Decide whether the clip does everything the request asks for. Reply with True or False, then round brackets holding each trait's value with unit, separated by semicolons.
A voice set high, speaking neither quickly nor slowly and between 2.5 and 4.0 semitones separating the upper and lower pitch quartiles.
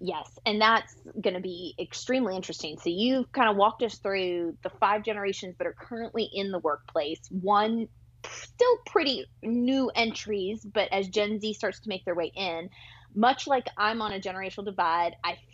True (205 Hz; 185 wpm; 3.6 semitones)